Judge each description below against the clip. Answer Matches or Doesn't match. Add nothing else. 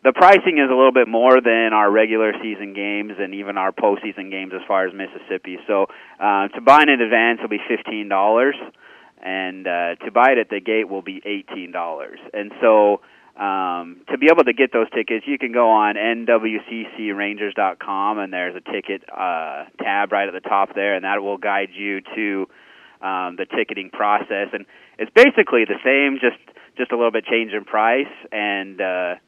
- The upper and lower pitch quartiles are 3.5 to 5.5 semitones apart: Doesn't match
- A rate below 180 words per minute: Doesn't match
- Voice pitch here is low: Matches